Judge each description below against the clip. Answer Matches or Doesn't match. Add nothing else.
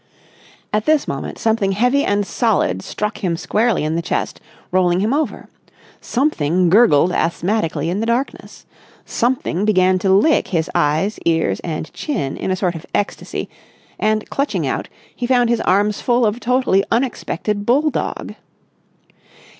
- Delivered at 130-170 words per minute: Matches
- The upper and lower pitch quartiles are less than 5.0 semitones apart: Doesn't match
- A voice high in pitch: Matches